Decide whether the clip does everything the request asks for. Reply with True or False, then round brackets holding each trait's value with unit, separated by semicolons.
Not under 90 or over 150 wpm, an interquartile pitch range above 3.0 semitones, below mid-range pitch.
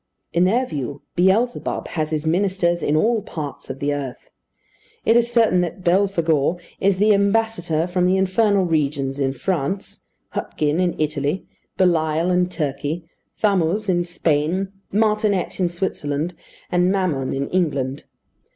False (140 wpm; 4.2 semitones; 175 Hz)